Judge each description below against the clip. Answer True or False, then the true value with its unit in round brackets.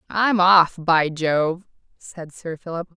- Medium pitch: True (170 Hz)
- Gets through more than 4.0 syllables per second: False (3.3 syllables/s)